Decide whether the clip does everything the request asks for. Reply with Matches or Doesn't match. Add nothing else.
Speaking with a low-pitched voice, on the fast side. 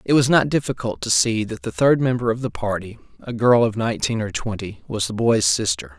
Matches